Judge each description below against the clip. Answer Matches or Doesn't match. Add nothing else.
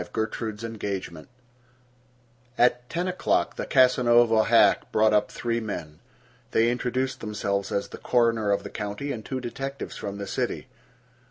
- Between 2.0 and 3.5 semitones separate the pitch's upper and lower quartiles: Matches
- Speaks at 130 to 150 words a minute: Matches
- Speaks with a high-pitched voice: Doesn't match